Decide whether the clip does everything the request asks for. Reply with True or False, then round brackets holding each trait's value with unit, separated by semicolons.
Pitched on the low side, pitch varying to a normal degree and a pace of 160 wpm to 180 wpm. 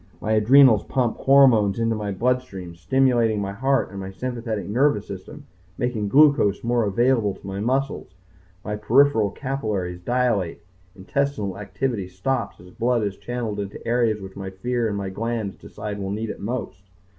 True (110 Hz; 4.1 semitones; 165 wpm)